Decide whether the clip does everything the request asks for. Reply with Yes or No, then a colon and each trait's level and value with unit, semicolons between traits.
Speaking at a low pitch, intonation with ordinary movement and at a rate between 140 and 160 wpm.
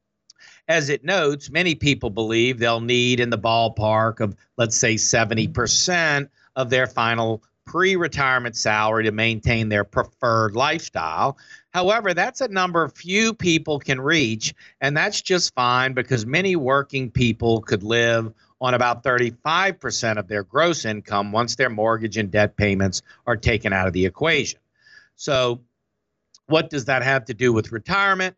Yes: low, 125 Hz; average, 4.3 semitones; average, 150 wpm